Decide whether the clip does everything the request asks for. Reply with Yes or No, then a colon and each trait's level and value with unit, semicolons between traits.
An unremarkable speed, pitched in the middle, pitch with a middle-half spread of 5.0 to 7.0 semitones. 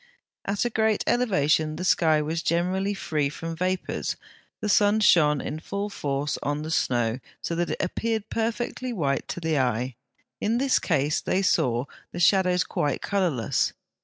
Yes: average, 165 wpm; medium, 170 Hz; wide, 5.4 semitones